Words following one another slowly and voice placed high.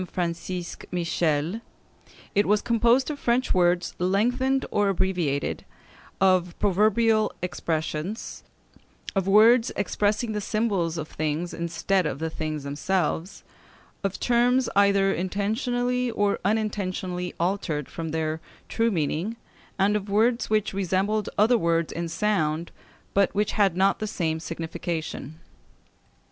Yes: slow, 120 wpm; high, 195 Hz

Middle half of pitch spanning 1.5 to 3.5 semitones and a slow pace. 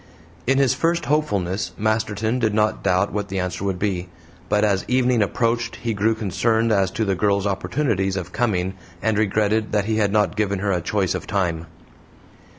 No: average, 2.7 semitones; average, 185 wpm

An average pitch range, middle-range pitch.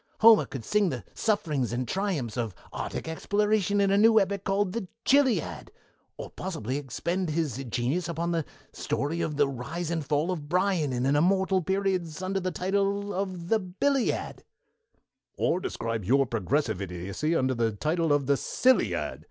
No: wide, 6.3 semitones; medium, 170 Hz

